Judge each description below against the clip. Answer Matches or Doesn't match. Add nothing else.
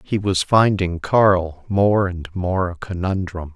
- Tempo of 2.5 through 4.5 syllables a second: Matches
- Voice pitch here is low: Matches